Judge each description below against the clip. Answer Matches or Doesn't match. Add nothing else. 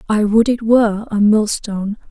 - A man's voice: Doesn't match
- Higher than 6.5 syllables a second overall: Doesn't match